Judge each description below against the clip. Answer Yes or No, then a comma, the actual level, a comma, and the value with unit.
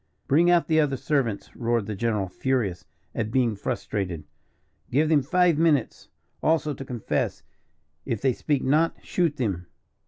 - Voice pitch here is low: Yes, low, 130 Hz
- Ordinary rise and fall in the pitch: No, wide, 6.0 semitones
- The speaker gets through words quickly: No, average, 150 wpm